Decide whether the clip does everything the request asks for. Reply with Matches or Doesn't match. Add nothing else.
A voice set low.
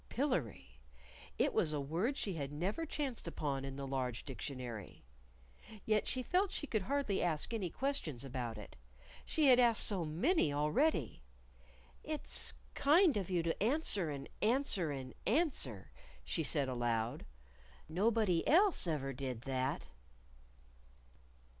Doesn't match